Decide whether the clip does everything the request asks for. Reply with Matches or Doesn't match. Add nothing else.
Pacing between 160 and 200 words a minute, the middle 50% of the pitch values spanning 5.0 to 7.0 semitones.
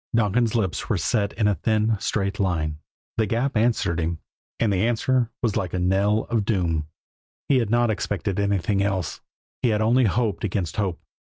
Doesn't match